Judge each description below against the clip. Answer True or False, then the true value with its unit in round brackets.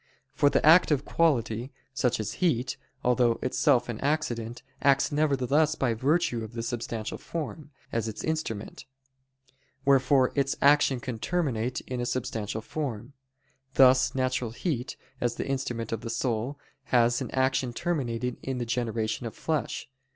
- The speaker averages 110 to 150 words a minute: True (145 wpm)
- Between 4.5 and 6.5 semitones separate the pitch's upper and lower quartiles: False (3.3 semitones)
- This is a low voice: True (125 Hz)